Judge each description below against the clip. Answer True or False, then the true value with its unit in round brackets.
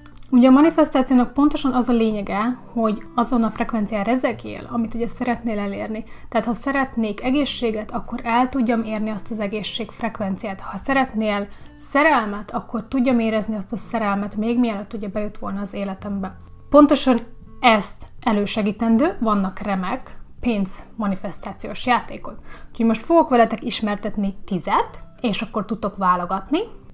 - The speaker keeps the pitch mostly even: False (3.0 semitones)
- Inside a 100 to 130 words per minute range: False (140 wpm)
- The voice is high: True (225 Hz)